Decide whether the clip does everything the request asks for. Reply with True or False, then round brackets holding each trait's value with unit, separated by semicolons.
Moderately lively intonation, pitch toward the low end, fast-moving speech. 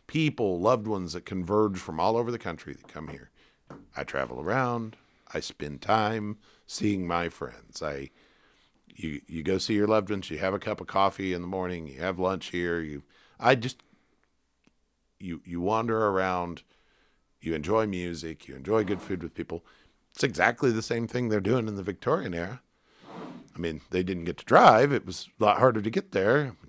False (4.3 semitones; 95 Hz; 190 wpm)